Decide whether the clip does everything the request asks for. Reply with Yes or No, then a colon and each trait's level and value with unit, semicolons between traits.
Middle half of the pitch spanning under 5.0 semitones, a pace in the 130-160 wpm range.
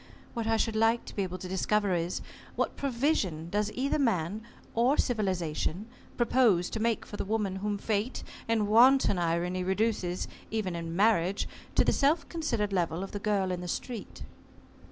No: average, 3.9 semitones; average, 175 wpm